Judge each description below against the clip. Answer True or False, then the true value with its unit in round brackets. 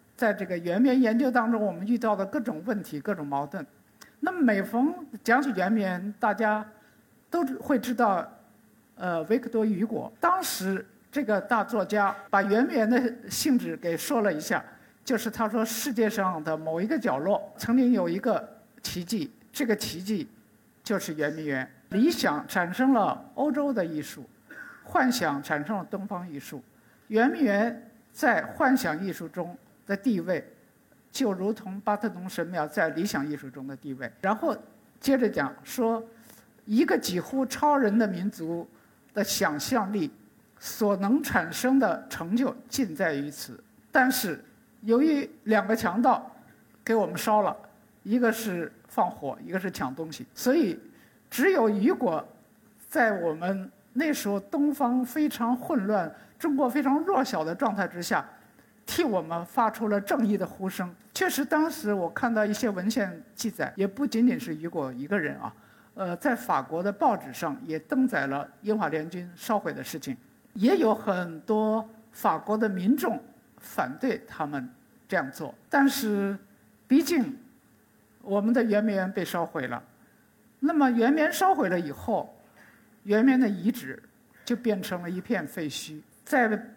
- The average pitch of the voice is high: True (220 Hz)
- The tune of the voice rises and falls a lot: False (5.0 semitones)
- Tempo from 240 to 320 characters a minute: False (230 characters per minute)